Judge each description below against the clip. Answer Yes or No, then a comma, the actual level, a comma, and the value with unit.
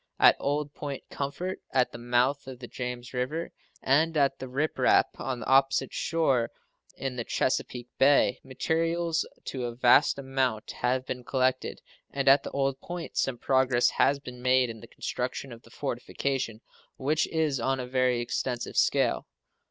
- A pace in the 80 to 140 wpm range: No, average, 165 wpm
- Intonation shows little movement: Yes, narrow, 2.1 semitones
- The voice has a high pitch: No, low, 130 Hz